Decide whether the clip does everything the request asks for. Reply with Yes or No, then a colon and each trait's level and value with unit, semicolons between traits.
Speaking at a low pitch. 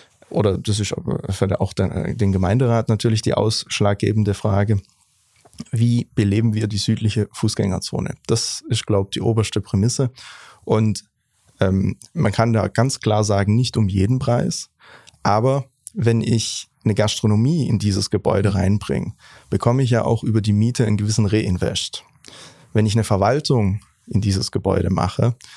Yes: low, 110 Hz